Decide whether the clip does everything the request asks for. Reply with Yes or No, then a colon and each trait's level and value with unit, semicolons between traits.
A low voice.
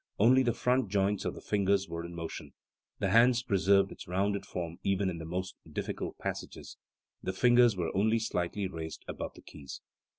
Yes: very low, 95 Hz